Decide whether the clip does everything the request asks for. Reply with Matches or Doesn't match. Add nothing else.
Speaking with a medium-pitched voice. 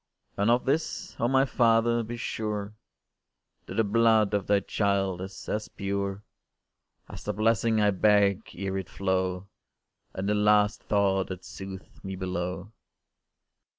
Doesn't match